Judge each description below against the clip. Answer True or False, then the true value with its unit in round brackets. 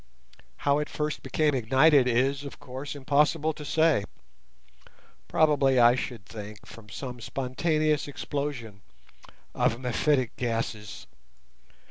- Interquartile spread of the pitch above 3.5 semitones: True (4.1 semitones)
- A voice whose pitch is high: False (130 Hz)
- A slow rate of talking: True (105 wpm)